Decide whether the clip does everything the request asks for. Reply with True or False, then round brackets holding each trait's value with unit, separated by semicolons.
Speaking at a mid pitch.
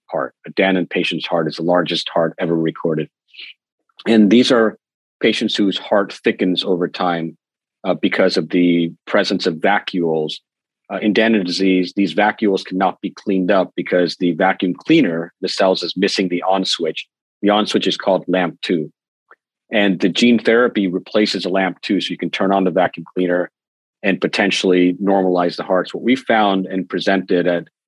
False (95 Hz)